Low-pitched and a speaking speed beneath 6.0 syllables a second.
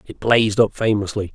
Yes: low, 105 Hz; 5.7 syllables/s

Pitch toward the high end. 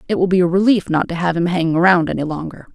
No: medium, 175 Hz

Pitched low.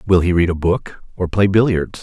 Yes: very low, 90 Hz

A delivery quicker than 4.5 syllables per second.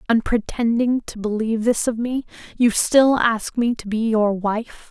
No: 4.3 syllables/s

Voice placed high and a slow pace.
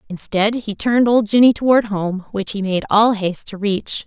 No: high, 210 Hz; fast, 205 wpm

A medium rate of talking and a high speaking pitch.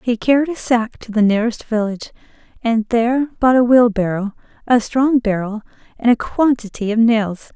Yes: average, 165 wpm; high, 230 Hz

